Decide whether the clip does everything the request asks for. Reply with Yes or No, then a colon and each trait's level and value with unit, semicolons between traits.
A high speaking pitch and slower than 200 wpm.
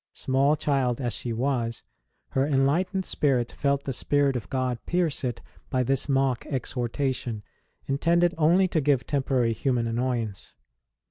No: low, 135 Hz; average, 140 wpm